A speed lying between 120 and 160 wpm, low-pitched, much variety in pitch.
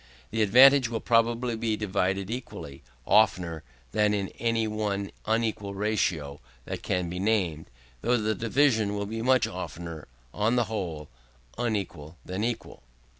No: average, 140 wpm; low, 105 Hz; average, 3.7 semitones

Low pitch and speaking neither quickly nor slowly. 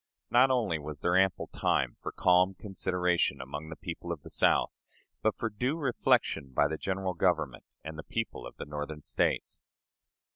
Yes: very low, 90 Hz; average, 175 wpm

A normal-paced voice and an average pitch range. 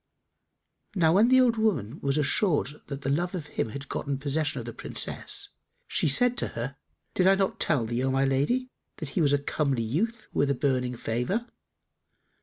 No: average, 195 wpm; wide, 5.9 semitones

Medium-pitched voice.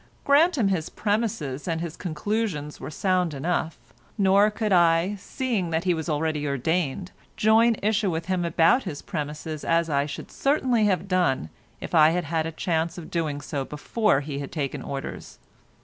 Yes: medium, 170 Hz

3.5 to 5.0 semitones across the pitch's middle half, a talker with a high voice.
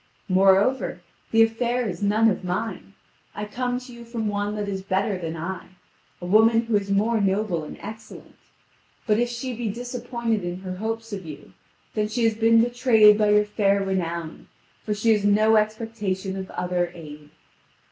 No: average, 3.0 semitones; high, 210 Hz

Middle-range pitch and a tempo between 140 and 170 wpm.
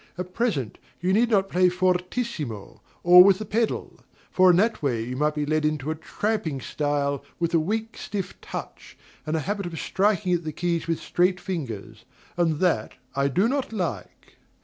No: medium, 175 Hz; average, 185 wpm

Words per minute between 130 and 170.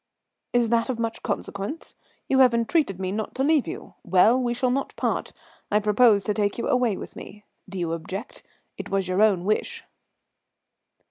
No: average, 185 wpm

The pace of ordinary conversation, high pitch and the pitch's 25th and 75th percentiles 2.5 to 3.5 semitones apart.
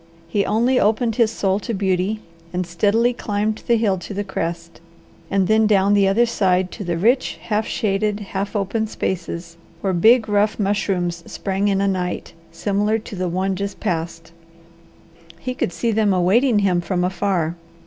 Yes: average, 170 wpm; high, 200 Hz; average, 2.9 semitones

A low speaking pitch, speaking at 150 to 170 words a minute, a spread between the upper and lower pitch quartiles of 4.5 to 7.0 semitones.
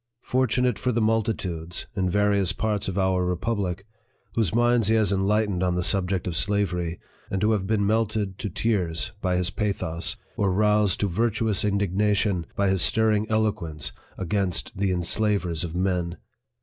No: low, 100 Hz; average, 165 wpm; average, 3.0 semitones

